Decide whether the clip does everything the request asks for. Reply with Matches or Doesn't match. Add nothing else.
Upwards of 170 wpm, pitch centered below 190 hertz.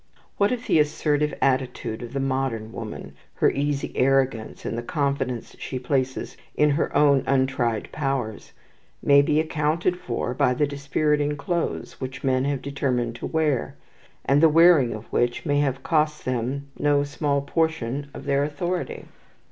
Doesn't match